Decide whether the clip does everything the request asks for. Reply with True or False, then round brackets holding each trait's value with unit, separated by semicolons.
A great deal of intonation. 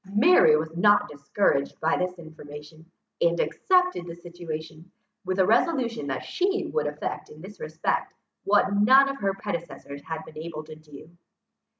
True (6.5 semitones)